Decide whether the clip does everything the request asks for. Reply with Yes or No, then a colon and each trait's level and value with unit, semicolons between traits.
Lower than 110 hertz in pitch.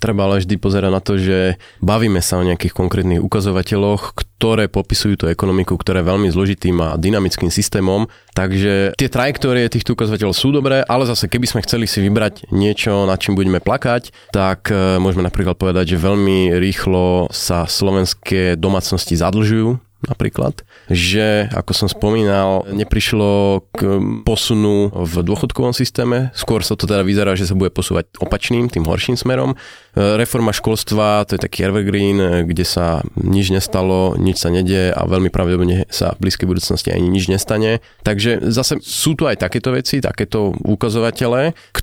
Yes: low, 100 Hz